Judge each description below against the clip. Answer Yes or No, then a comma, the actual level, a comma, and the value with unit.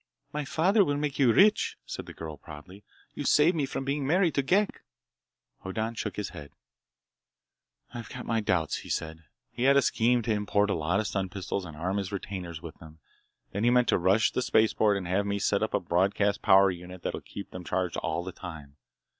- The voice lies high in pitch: No, low, 100 Hz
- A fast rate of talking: Yes, fast, 215 wpm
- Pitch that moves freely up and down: Yes, wide, 5.7 semitones